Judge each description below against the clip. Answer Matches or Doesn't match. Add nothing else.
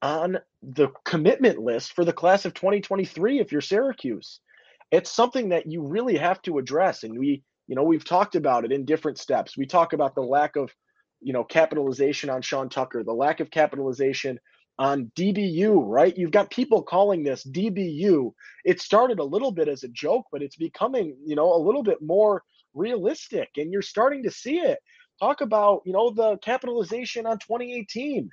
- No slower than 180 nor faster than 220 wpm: Matches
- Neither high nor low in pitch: Matches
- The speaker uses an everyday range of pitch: Doesn't match